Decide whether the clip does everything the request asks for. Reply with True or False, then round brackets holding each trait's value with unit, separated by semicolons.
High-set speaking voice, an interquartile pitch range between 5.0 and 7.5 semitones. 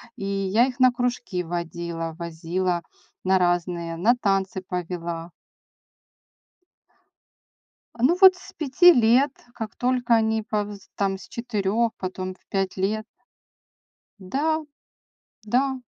True (200 Hz; 5.3 semitones)